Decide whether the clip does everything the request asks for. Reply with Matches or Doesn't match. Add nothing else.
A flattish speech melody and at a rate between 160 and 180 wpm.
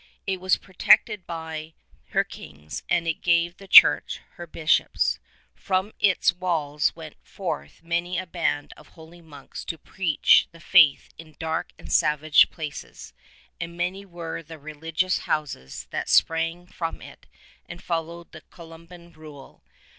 Doesn't match